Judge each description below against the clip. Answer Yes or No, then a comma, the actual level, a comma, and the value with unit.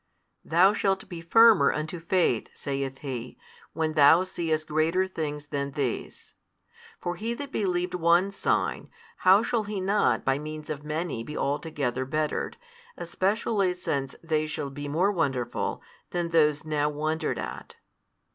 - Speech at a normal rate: Yes, average, 145 wpm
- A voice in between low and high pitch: Yes, medium, 155 Hz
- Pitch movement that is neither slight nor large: Yes, average, 4.1 semitones